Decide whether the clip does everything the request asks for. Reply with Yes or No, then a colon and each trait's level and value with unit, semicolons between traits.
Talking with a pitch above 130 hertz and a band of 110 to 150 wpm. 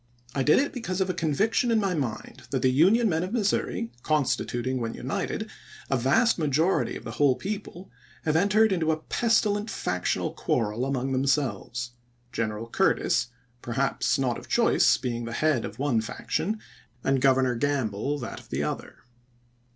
No: medium, 140 Hz; average, 165 wpm